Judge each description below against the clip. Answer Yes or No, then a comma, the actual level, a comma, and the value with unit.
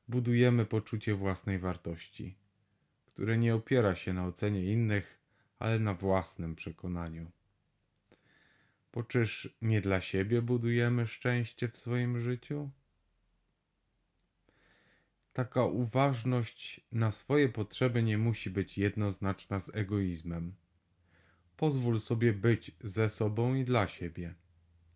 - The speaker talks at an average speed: No, slow, 105 wpm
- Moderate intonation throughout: Yes, average, 4.3 semitones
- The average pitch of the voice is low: Yes, low, 110 Hz